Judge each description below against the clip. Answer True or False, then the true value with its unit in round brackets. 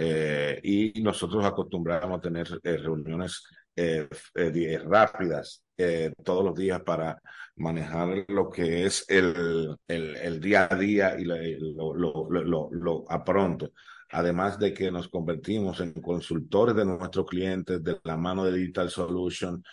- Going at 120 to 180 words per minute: True (150 wpm)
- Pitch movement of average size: False (2.3 semitones)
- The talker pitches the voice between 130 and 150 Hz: False (90 Hz)